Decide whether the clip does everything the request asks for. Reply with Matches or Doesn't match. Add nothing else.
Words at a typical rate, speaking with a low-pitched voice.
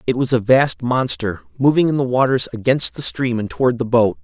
Doesn't match